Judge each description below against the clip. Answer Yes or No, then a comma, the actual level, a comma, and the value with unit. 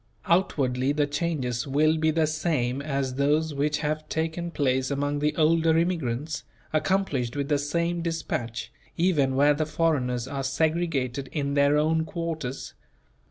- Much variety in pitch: No, average, 2.9 semitones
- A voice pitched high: No, medium, 150 Hz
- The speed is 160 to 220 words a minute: No, average, 145 wpm